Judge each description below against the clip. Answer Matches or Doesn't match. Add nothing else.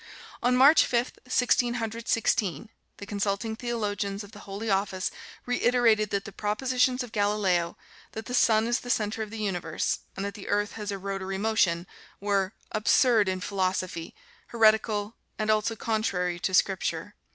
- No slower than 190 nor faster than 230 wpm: Doesn't match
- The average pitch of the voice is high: Matches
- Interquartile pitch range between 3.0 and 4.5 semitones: Doesn't match